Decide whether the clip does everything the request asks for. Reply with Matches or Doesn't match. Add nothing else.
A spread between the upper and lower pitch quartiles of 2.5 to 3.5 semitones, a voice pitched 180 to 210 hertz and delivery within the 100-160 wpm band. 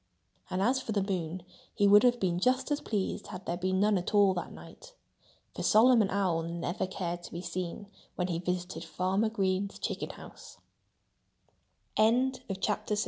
Matches